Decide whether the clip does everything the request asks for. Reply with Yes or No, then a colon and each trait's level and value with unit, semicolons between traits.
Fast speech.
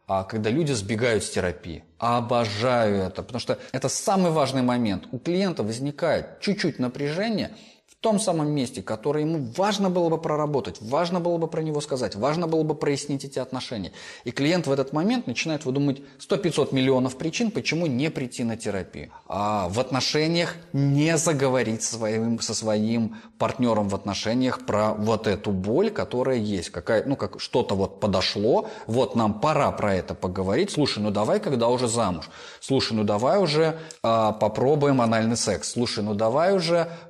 Yes: fast, 170 wpm